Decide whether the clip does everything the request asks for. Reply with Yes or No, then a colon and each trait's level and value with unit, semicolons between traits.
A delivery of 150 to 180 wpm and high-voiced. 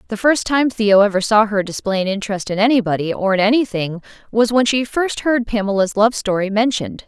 No: fast, 205 wpm; high, 215 Hz